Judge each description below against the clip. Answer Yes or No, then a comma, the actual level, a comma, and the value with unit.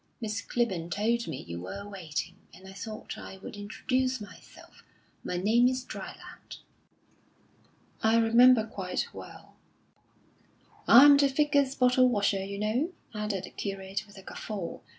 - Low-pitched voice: No, high, 210 Hz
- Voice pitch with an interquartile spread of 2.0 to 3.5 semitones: No, average, 4.4 semitones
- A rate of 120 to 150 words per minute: Yes, average, 140 wpm